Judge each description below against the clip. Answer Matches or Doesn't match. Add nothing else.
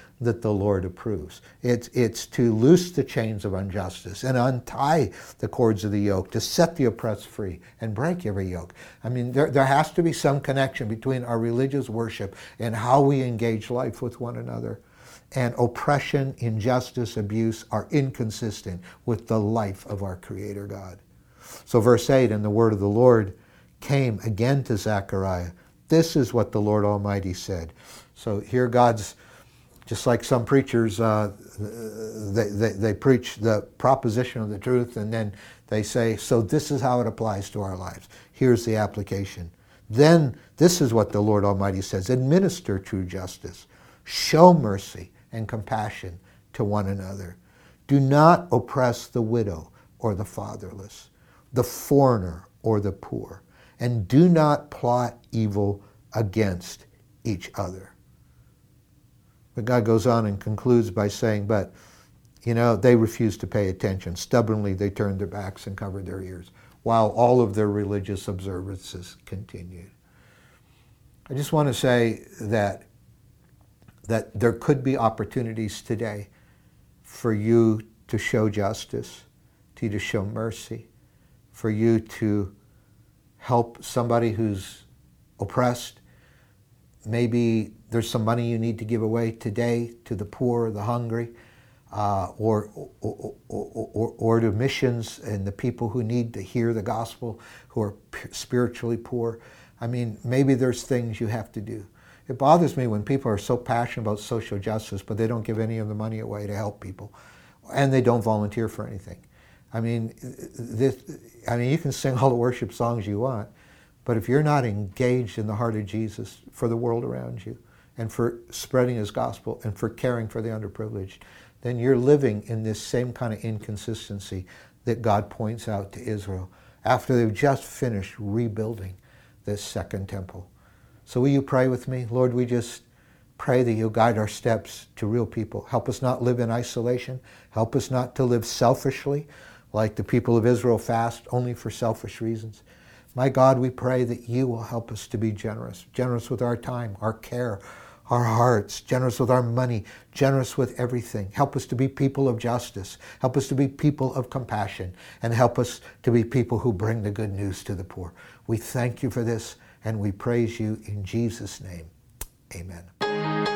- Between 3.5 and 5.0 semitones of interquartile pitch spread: Doesn't match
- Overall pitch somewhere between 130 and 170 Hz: Doesn't match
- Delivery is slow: Doesn't match